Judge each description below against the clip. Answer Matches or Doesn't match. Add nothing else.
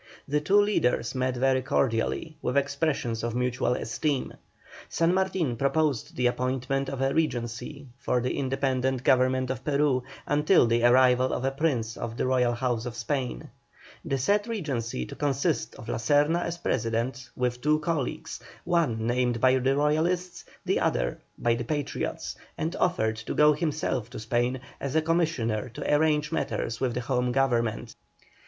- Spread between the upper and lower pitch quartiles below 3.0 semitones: Doesn't match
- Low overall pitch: Matches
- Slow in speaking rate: Doesn't match